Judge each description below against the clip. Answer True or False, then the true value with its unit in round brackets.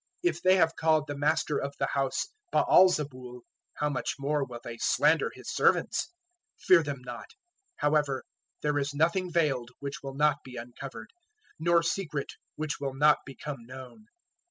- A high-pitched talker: False (145 Hz)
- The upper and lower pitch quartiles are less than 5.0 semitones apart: True (2.9 semitones)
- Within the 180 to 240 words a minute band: False (165 wpm)